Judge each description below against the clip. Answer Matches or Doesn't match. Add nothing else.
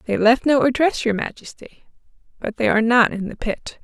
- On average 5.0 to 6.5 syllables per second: Matches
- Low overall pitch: Doesn't match